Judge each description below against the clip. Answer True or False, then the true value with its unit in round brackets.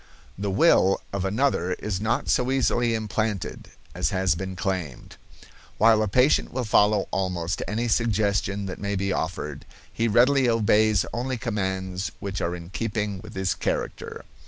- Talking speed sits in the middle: True (155 wpm)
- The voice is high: False (100 Hz)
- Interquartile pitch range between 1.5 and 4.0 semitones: True (3.2 semitones)